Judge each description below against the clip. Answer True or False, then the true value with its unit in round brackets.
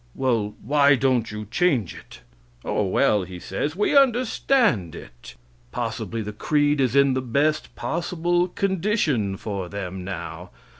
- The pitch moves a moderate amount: False (8.4 semitones)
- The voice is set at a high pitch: False (130 Hz)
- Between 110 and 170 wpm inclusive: True (140 wpm)